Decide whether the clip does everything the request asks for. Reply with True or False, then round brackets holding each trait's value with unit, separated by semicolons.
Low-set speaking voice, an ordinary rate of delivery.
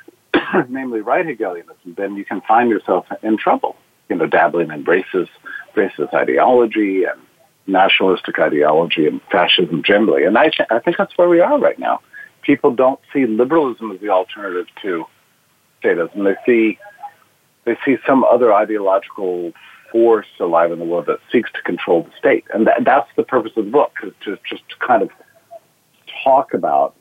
True (120 Hz; 170 wpm)